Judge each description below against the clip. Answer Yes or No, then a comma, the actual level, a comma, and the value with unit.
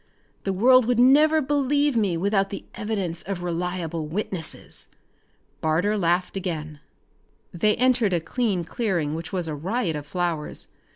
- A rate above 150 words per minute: No, average, 140 wpm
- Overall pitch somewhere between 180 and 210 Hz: Yes, high, 190 Hz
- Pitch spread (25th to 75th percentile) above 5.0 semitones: Yes, wide, 5.5 semitones